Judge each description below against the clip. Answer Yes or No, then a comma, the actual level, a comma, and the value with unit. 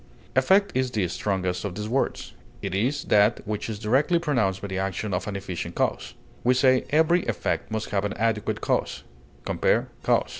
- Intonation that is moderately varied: Yes, average, 4.9 semitones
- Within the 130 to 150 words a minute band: No, average, 185 wpm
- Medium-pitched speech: No, low, 110 Hz